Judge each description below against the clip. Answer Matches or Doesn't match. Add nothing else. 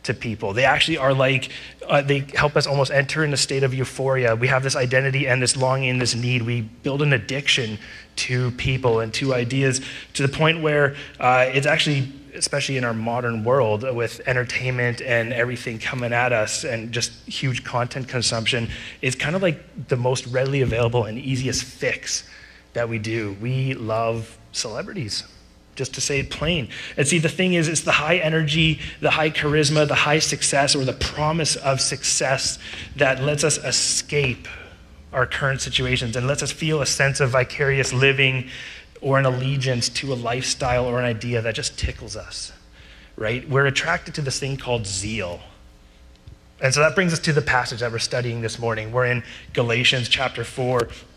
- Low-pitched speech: Matches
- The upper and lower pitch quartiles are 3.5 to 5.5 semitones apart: Doesn't match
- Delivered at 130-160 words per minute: Doesn't match